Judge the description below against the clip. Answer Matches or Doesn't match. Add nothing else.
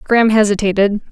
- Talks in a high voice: Matches